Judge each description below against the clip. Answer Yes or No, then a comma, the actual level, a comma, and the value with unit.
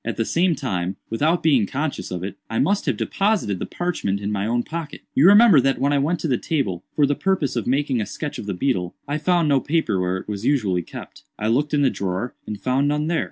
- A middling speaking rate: No, fast, 250 wpm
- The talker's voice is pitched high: No, low, 135 Hz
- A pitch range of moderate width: No, wide, 7.0 semitones